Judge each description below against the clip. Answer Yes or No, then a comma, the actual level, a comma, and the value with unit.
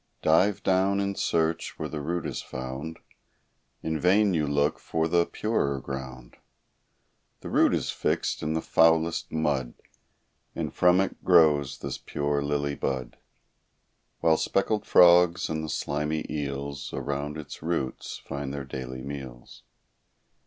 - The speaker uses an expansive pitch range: No, average, 3.2 semitones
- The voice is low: Yes, very low, 75 Hz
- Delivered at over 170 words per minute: No, average, 140 wpm